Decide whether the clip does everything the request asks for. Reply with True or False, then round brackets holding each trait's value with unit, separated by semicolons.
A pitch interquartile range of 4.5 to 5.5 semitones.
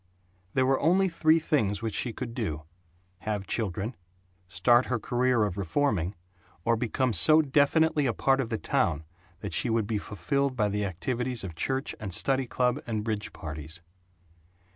True (4.8 semitones)